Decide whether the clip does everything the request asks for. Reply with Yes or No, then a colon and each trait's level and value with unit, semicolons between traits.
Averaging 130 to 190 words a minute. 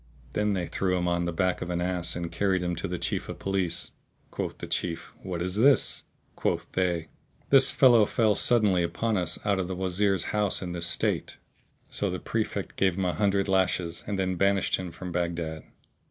No: average, 200 wpm